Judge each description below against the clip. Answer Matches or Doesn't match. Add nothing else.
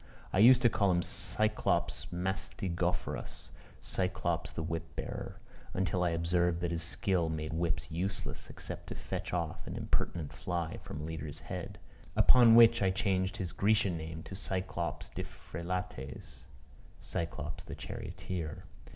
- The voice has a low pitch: Matches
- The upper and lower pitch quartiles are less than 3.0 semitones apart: Matches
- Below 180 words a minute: Matches